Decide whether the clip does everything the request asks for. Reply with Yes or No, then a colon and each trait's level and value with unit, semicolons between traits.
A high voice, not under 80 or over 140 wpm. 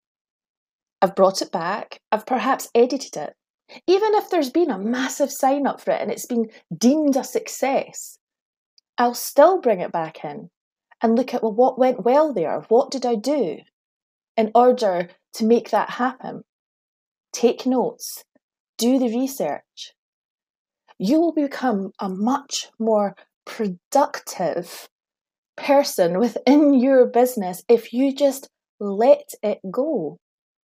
Yes: very high, 250 Hz; slow, 135 wpm